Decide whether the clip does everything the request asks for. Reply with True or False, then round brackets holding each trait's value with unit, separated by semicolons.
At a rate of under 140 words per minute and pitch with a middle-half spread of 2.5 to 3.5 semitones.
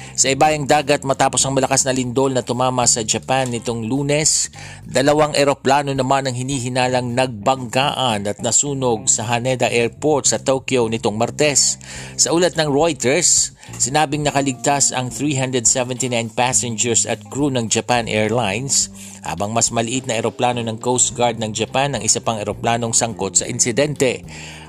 False (145 wpm; 2.8 semitones)